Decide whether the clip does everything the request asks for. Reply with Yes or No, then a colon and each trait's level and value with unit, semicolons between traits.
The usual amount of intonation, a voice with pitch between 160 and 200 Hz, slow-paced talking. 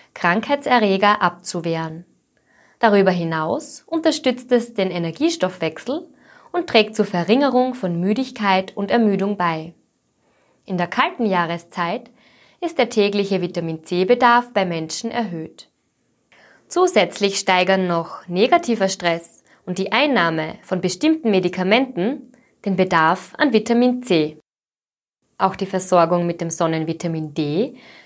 No: wide, 5.8 semitones; high, 190 Hz; slow, 105 wpm